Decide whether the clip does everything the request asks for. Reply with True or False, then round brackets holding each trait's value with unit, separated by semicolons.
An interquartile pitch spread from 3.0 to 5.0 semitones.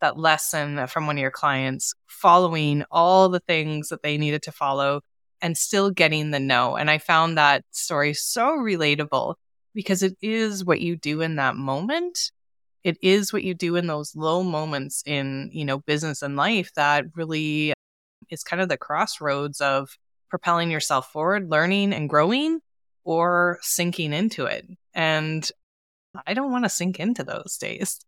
True (3.9 semitones)